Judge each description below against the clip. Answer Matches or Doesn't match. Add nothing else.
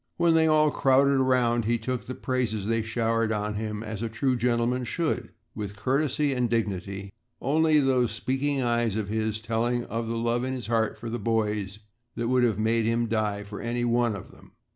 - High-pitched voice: Doesn't match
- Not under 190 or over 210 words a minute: Matches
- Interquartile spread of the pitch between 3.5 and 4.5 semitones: Doesn't match